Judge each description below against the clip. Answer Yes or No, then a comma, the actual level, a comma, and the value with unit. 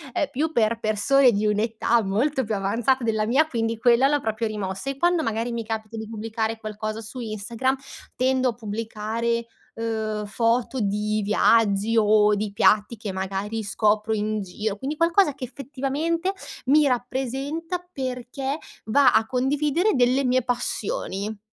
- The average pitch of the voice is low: No, high, 230 Hz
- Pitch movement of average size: Yes, average, 3.6 semitones